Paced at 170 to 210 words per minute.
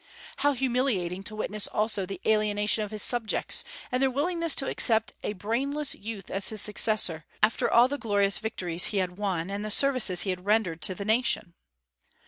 Yes: average, 185 wpm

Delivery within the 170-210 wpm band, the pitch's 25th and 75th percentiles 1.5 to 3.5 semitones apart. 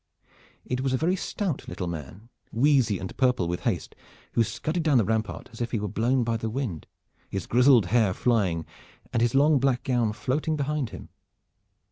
No: average, 185 wpm; average, 4.3 semitones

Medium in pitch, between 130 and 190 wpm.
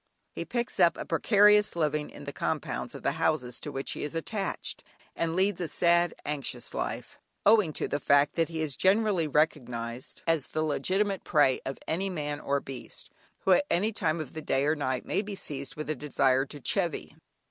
No: medium, 155 Hz; average, 200 wpm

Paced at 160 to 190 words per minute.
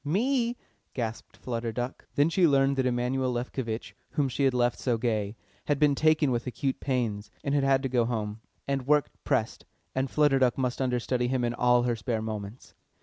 No: average, 200 wpm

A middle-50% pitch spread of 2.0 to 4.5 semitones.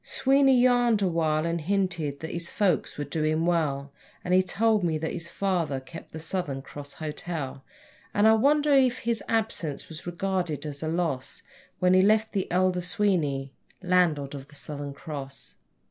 No: average, 4.9 semitones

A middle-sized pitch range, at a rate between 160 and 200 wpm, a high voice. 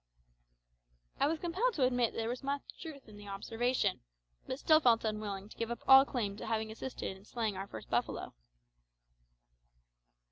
Yes: average, 4.1 semitones; average, 175 wpm; high, 235 Hz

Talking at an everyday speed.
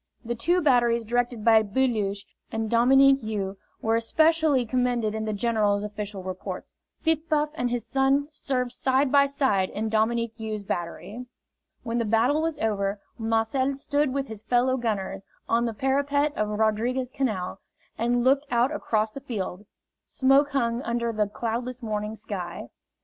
Yes: average, 155 wpm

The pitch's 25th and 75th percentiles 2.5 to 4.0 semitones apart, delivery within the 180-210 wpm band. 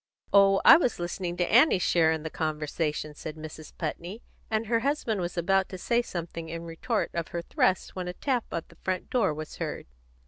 No: average, 4.7 semitones; fast, 205 wpm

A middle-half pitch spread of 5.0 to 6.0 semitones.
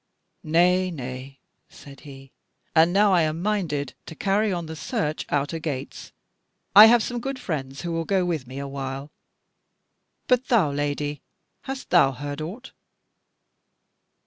Yes: wide, 5.4 semitones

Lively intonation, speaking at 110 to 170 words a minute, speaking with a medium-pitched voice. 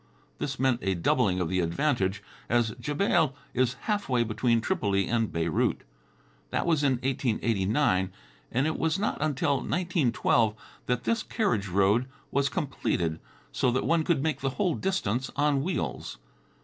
No: wide, 6.3 semitones; average, 150 wpm; low, 130 Hz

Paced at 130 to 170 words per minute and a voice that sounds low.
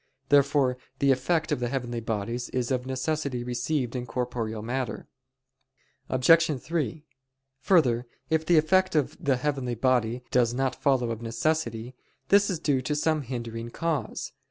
Yes: average, 150 wpm; low, 130 Hz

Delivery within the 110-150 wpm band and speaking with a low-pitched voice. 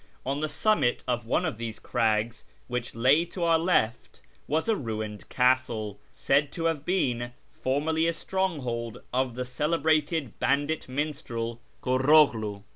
Yes: average, 140 wpm; low, 130 Hz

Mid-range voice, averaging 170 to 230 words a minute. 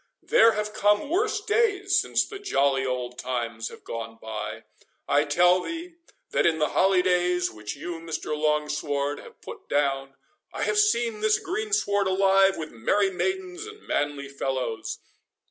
No: medium, 180 Hz; average, 145 wpm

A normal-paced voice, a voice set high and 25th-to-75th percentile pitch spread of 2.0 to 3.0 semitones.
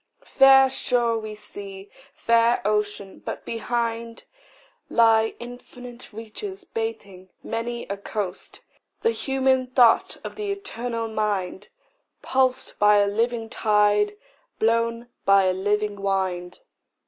No: slow, 110 wpm; high, 225 Hz; average, 2.7 semitones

